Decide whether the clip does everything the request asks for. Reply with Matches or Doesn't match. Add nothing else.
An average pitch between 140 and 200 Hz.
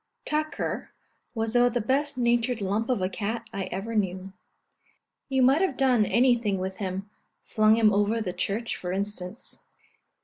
Doesn't match